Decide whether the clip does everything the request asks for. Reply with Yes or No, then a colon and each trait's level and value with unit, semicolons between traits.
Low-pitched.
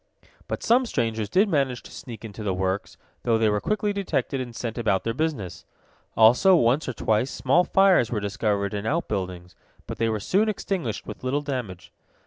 Yes: low, 120 Hz